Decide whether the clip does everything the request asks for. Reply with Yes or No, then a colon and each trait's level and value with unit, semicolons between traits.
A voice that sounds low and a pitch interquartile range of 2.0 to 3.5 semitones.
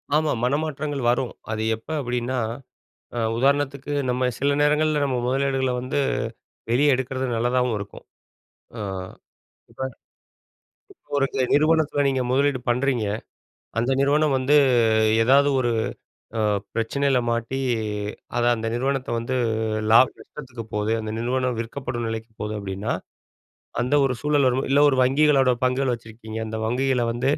Yes: low, 130 Hz; average, 2.8 semitones